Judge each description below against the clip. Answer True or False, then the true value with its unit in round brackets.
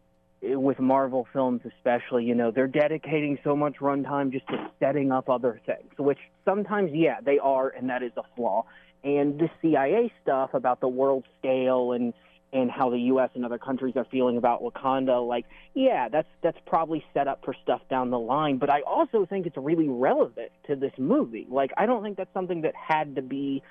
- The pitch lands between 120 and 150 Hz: True (135 Hz)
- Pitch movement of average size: True (3.4 semitones)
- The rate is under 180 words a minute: False (200 wpm)